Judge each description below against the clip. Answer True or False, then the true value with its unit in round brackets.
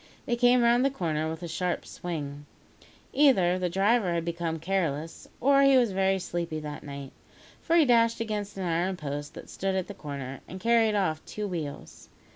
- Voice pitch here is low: False (185 Hz)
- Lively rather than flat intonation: True (6.2 semitones)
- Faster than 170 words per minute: True (190 wpm)